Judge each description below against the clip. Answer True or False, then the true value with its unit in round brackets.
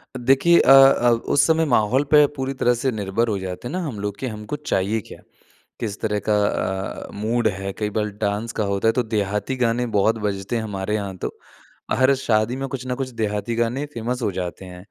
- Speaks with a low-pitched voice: True (110 Hz)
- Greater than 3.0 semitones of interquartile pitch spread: True (3.8 semitones)